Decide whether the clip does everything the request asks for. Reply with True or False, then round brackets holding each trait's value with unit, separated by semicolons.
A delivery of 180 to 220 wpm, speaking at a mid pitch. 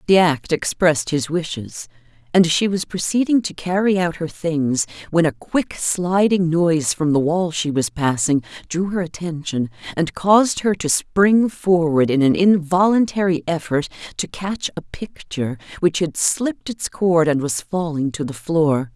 False (170 wpm; 165 Hz)